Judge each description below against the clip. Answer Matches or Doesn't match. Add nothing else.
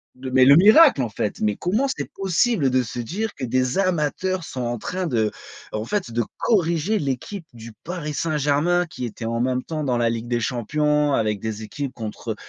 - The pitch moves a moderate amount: Doesn't match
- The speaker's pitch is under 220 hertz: Matches